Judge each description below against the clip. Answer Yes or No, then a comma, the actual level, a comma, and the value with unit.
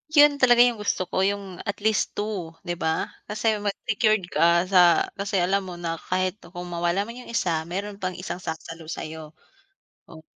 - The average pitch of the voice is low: No, medium, 185 Hz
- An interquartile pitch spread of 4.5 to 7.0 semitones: No, average, 3.3 semitones